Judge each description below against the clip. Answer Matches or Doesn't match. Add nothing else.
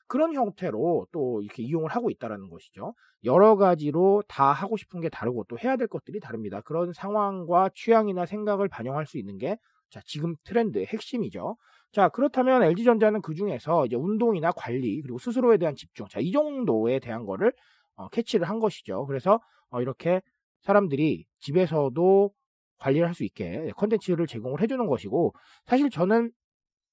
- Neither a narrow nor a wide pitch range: Doesn't match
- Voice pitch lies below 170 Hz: Doesn't match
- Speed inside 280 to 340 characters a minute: Doesn't match